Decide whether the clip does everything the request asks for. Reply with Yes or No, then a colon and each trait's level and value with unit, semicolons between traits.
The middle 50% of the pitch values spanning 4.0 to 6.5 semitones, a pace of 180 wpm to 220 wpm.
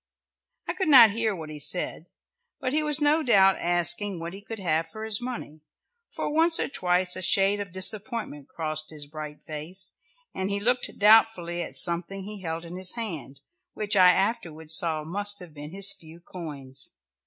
Yes: average, 4.7 semitones; average, 185 wpm